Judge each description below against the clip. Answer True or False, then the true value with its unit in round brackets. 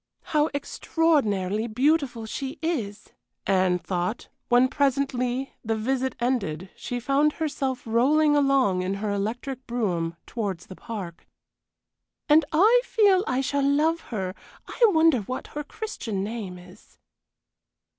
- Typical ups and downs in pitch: False (6.2 semitones)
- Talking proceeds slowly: True (125 wpm)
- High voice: True (250 Hz)